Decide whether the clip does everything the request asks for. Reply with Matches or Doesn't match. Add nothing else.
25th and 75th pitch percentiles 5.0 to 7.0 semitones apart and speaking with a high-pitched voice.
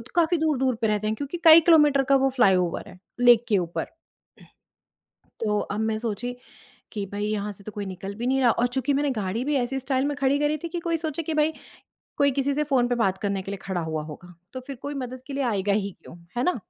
Matches